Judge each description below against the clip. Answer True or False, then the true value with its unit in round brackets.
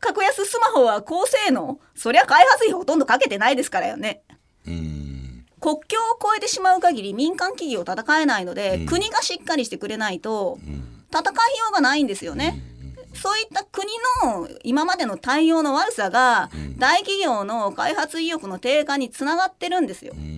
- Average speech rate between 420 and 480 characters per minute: False (340 characters per minute)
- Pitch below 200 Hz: False (305 Hz)